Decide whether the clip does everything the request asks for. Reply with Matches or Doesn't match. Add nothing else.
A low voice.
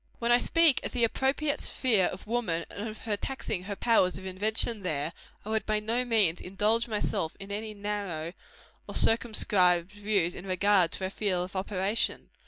Doesn't match